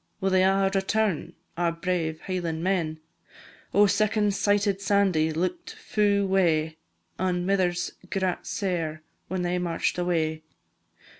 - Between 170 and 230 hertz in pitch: Yes, medium, 185 Hz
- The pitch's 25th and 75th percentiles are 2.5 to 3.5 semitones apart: Yes, average, 3.0 semitones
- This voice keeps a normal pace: No, slow, 125 wpm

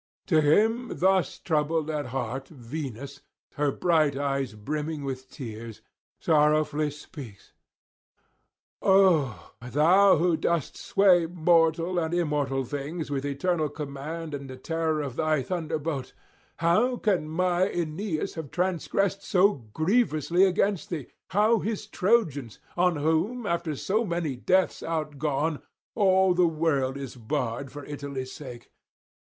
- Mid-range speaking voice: Yes, medium, 155 Hz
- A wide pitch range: No, average, 4.1 semitones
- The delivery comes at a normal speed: No, slow, 125 wpm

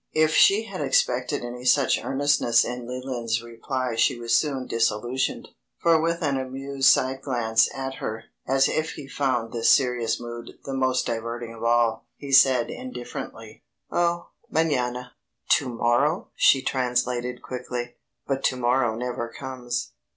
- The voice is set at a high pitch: No, low, 125 Hz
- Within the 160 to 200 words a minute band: No, average, 150 wpm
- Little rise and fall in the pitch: Yes, narrow, 2.3 semitones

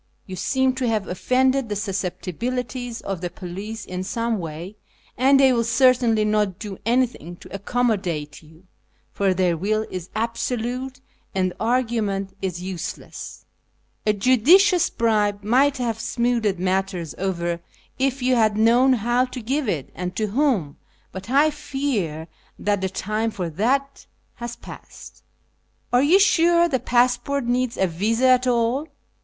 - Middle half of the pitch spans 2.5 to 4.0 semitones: No, average, 5.0 semitones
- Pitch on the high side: Yes, high, 225 Hz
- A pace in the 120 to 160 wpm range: Yes, average, 150 wpm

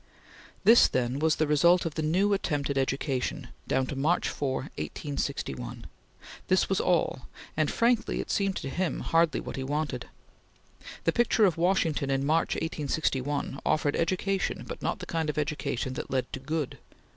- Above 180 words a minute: No, average, 170 wpm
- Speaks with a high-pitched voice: No, medium, 150 Hz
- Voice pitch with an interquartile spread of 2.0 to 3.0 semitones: No, average, 4.0 semitones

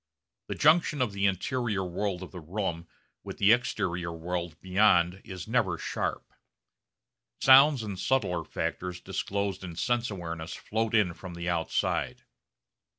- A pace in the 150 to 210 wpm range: No, average, 140 wpm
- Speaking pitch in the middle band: No, very low, 95 Hz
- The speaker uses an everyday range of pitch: Yes, average, 4.0 semitones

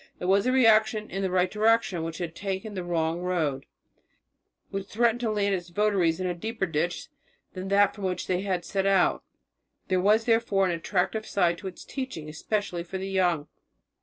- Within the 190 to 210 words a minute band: Yes, average, 195 wpm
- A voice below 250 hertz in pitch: Yes, high, 190 Hz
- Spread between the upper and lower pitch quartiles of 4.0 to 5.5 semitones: No, average, 3.3 semitones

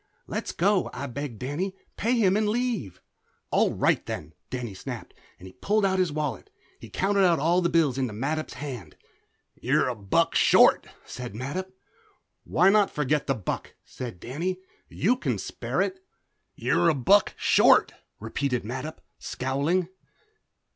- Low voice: No, medium, 150 Hz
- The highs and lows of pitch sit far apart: Yes, wide, 6.9 semitones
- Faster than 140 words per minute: Yes, average, 150 wpm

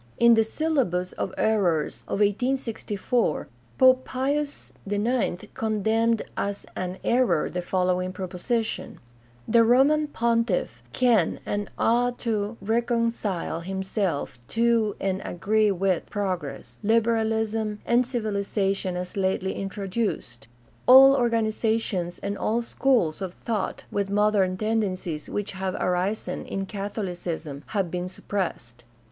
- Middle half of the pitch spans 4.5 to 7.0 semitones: No, average, 3.9 semitones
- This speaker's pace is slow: Yes, slow, 115 wpm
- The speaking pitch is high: Yes, high, 205 Hz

